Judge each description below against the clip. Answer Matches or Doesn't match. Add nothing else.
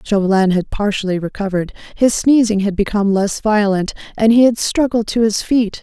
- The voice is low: Doesn't match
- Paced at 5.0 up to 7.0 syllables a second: Matches